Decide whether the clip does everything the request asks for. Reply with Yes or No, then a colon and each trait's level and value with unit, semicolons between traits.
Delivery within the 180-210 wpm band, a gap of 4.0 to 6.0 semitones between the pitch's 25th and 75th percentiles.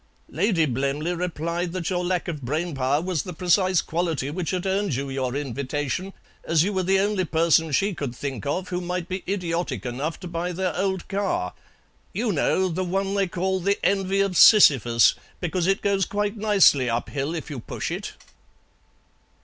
Yes: average, 185 wpm; average, 4.5 semitones